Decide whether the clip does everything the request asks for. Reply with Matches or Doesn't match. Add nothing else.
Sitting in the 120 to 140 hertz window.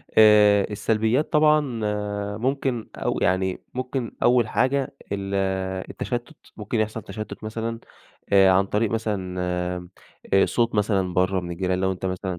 Doesn't match